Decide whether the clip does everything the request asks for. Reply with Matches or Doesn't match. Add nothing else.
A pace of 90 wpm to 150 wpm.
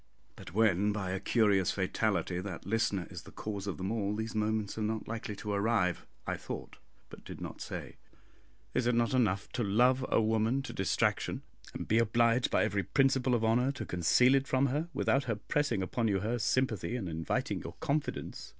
Doesn't match